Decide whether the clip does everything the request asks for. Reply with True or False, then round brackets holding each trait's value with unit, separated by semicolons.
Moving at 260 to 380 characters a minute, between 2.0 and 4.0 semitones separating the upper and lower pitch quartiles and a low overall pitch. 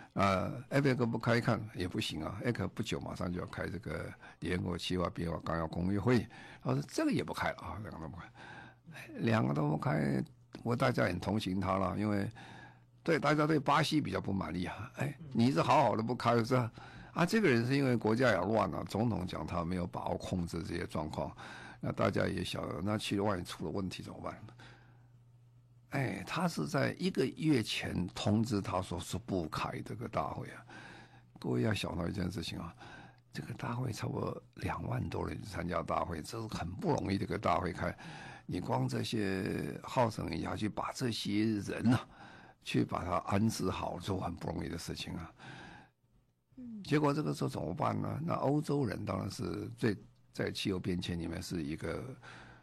False (280 characters per minute; 5.5 semitones; 105 Hz)